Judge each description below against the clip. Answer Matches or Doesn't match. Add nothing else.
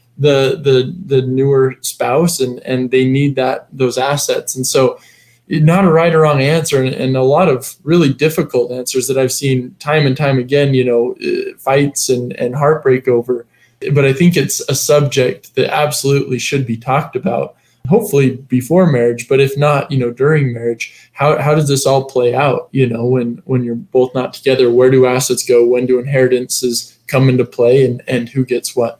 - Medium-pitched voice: Doesn't match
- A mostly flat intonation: Matches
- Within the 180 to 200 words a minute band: Matches